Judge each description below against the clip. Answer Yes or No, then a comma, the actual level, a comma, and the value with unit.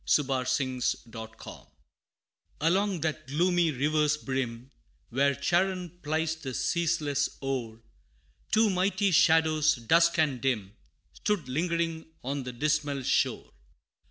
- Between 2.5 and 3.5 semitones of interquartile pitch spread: No, average, 4.2 semitones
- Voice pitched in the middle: Yes, medium, 150 Hz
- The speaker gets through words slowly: Yes, slow, 115 wpm